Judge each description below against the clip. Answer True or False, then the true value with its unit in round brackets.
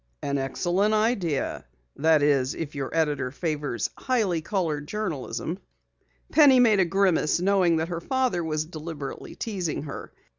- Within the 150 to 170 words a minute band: False (140 wpm)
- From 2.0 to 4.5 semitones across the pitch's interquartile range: False (5.1 semitones)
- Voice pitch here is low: False (165 Hz)